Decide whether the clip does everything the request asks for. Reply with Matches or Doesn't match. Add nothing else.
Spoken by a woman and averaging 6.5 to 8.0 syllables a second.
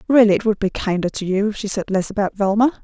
Matches